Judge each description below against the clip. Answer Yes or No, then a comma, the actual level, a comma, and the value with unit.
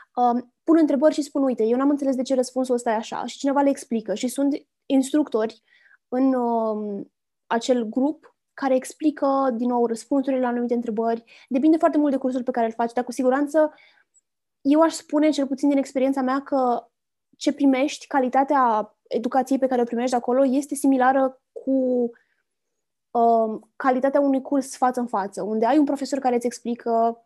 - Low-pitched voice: No, very high, 260 Hz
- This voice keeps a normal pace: No, fast, 175 wpm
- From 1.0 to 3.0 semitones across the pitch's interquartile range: Yes, average, 2.7 semitones